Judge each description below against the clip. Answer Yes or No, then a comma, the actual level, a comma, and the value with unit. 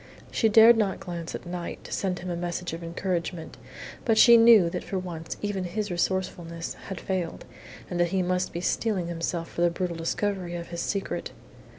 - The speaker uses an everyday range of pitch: No, narrow, 2.2 semitones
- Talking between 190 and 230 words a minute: Yes, average, 195 wpm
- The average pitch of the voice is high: No, medium, 180 Hz